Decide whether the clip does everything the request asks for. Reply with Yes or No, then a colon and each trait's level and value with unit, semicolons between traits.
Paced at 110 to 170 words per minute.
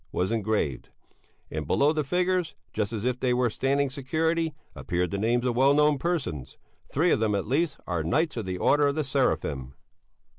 No: average, 190 wpm